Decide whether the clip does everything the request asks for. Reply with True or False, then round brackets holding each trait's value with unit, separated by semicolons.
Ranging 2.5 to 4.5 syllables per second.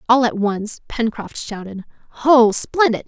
True (4.1 syllables/s)